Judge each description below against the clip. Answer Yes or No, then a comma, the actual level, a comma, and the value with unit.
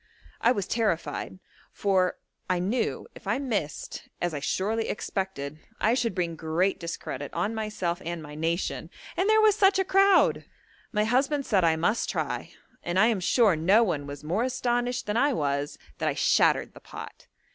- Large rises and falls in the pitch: Yes, wide, 6.3 semitones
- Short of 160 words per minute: No, average, 180 wpm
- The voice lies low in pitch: No, high, 195 Hz